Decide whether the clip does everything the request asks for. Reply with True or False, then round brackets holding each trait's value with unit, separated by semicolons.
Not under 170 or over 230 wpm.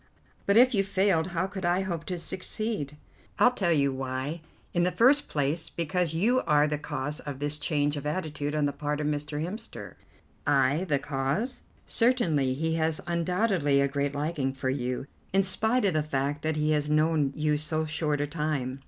True (190 wpm)